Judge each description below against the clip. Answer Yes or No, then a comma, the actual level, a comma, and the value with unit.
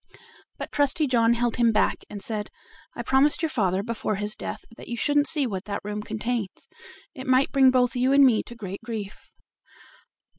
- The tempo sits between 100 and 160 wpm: No, average, 190 wpm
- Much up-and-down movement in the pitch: No, average, 3.9 semitones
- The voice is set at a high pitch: Yes, high, 235 Hz